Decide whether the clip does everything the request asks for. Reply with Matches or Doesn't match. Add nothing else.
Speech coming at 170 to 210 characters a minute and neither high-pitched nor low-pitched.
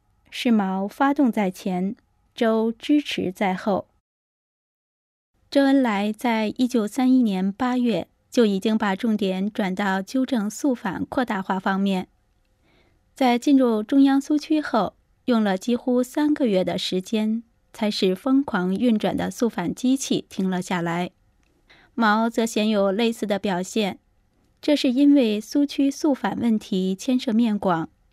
Doesn't match